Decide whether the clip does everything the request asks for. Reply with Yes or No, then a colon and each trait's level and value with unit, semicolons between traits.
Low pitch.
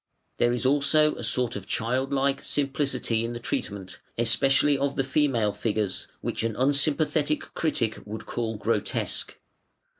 Yes: low, 130 Hz